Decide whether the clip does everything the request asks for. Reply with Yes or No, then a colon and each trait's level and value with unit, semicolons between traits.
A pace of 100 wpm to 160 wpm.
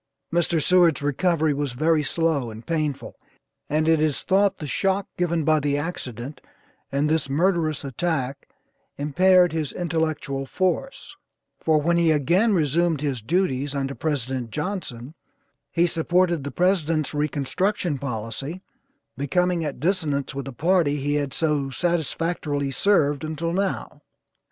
Yes: slow, 135 wpm